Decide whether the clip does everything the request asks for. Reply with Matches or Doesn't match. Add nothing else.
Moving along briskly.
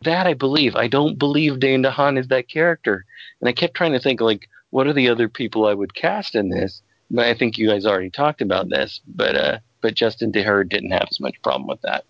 Matches